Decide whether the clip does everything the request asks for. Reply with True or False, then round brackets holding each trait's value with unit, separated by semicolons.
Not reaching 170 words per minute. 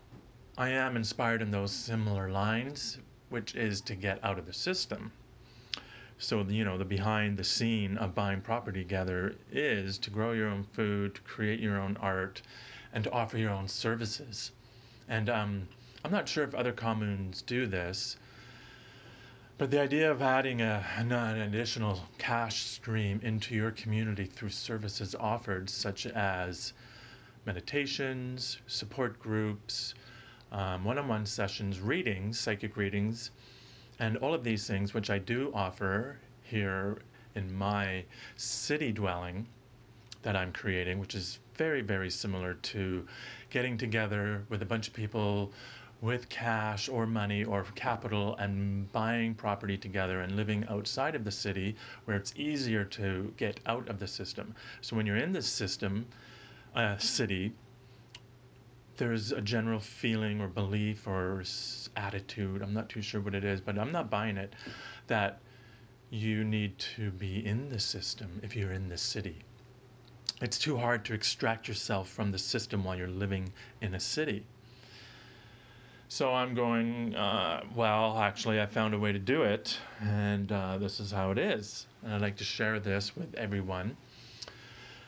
True (155 wpm)